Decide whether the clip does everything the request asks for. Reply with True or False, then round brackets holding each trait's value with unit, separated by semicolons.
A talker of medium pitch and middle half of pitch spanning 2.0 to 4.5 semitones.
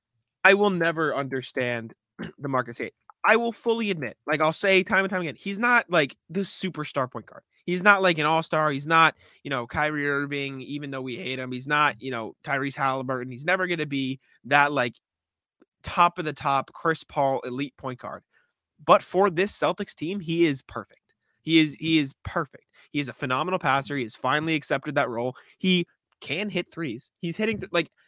False (150 Hz; 5.1 semitones)